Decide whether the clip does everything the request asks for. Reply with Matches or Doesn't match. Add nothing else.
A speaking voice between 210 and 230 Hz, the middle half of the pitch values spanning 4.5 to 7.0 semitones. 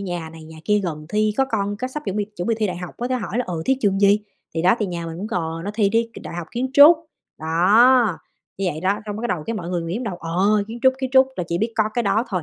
Doesn't match